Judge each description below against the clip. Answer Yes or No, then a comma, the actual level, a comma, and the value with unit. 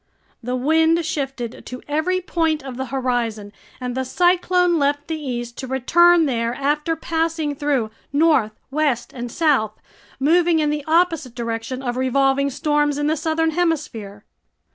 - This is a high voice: Yes, very high, 285 Hz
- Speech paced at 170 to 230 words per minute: No, average, 150 wpm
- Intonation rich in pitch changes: No, average, 4.3 semitones